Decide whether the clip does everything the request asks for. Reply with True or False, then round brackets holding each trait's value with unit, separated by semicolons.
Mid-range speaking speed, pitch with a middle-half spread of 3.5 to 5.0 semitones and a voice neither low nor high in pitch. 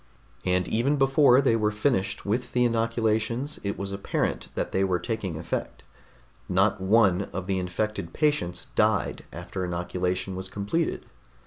False (145 wpm; 3.9 semitones; 100 Hz)